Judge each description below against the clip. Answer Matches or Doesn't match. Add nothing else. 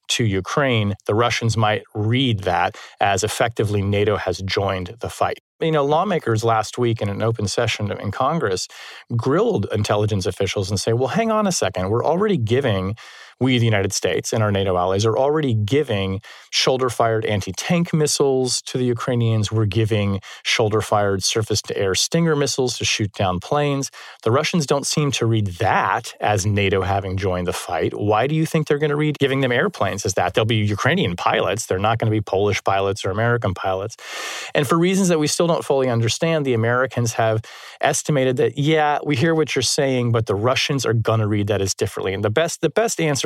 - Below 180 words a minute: Doesn't match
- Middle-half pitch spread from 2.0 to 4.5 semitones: Doesn't match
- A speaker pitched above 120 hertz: Doesn't match